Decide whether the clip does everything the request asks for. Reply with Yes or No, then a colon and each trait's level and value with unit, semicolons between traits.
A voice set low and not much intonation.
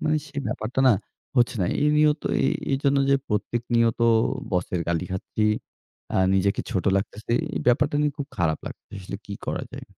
No: low, 115 Hz; wide, 6.3 semitones